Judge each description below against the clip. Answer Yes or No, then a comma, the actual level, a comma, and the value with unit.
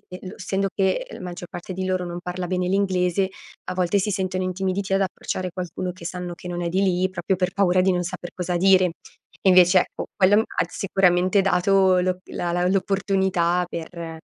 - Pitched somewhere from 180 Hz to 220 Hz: Yes, medium, 185 Hz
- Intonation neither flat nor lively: No, narrow, 1.3 semitones